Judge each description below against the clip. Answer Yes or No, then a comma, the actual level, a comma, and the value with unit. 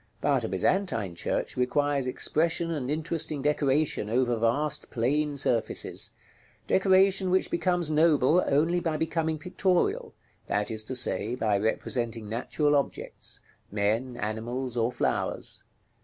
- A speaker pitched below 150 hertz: Yes, medium, 140 Hz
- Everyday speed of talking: No, slow, 125 wpm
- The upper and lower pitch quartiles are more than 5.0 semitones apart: Yes, wide, 5.4 semitones